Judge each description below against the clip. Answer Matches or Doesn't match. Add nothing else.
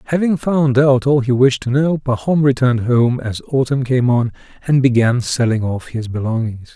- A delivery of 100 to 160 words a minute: Doesn't match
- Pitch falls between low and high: Doesn't match